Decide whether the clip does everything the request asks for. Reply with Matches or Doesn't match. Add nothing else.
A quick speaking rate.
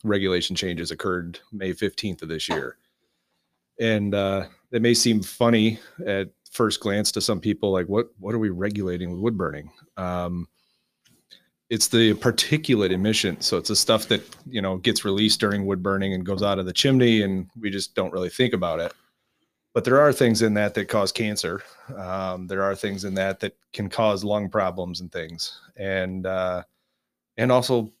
Doesn't match